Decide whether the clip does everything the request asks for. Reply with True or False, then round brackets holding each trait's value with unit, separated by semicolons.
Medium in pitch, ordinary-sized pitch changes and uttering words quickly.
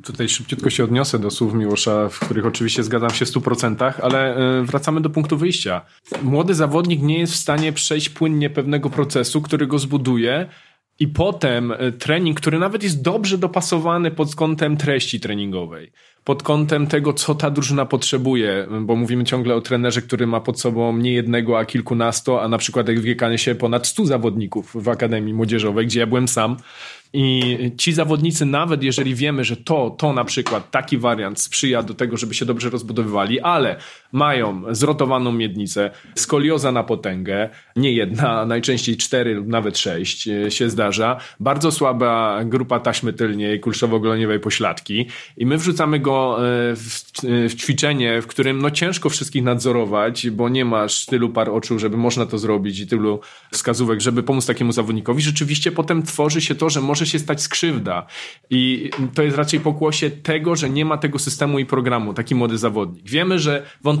False (125 Hz; 4.2 semitones; 170 wpm)